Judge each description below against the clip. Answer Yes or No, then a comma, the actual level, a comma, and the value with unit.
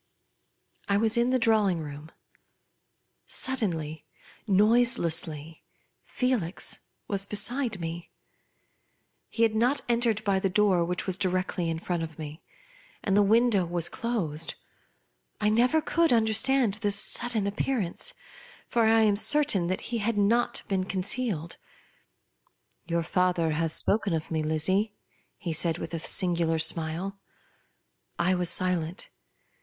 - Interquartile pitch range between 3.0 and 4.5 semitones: No, average, 5.1 semitones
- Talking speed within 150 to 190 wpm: No, slow, 135 wpm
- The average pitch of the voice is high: Yes, high, 195 Hz